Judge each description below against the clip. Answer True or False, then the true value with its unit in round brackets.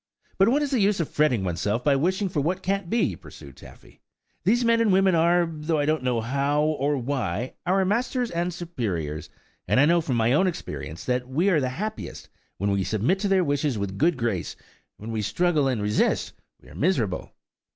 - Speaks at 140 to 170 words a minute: False (205 wpm)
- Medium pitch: True (150 Hz)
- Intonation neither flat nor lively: False (7.7 semitones)